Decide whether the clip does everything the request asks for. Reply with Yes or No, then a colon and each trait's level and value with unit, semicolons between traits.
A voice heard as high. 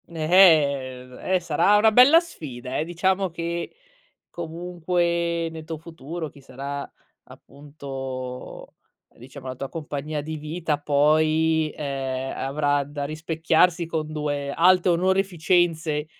No: medium, 155 Hz